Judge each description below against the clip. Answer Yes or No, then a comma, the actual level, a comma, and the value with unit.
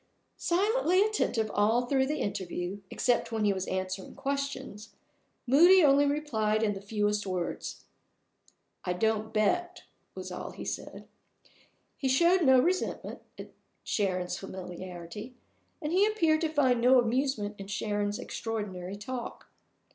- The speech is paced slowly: Yes, slow, 130 wpm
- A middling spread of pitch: No, wide, 5.9 semitones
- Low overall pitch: No, high, 225 Hz